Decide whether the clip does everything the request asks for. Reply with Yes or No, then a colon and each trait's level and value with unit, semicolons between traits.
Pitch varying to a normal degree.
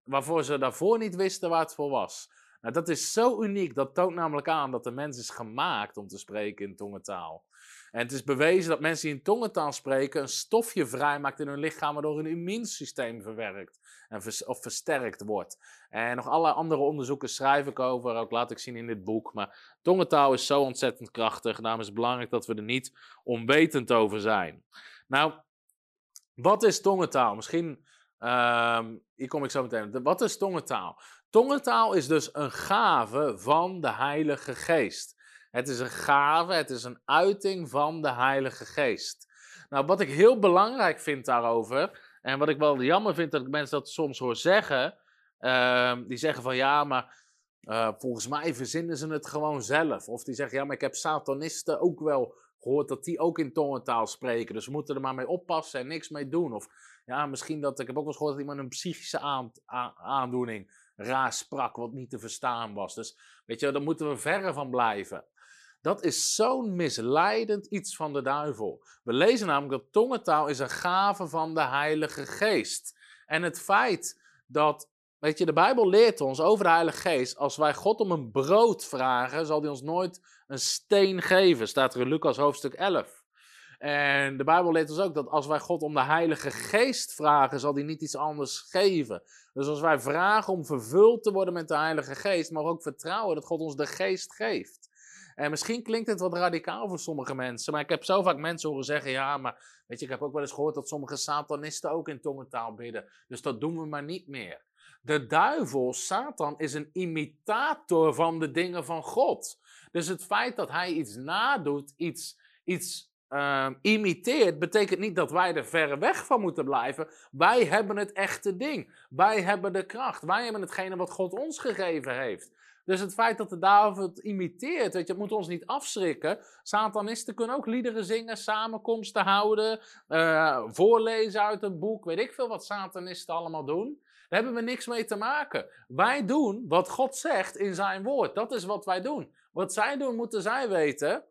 No: wide, 5.8 semitones